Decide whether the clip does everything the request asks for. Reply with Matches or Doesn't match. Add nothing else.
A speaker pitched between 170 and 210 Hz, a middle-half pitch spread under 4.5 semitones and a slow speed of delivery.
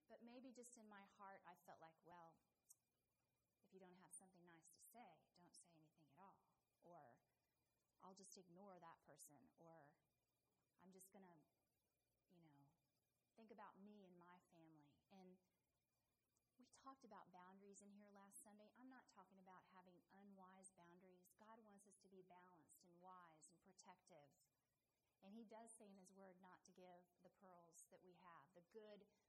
Doesn't match